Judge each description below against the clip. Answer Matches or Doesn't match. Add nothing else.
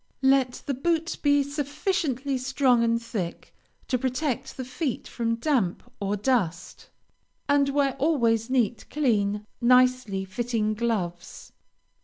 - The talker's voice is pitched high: Matches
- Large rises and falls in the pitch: Doesn't match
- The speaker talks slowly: Matches